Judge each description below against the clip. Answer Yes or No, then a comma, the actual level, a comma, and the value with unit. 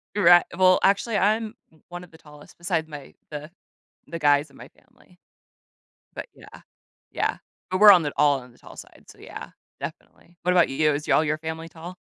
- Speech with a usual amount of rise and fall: Yes, average, 3.5 semitones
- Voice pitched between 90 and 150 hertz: No, medium, 165 Hz